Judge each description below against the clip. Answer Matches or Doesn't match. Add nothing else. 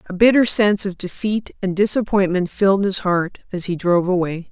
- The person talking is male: Doesn't match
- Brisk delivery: Doesn't match